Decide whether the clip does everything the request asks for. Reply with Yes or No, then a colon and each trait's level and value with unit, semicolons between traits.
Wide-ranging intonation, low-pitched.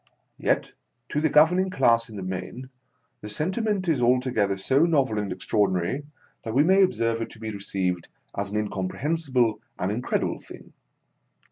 Yes: wide, 6.6 semitones; low, 115 Hz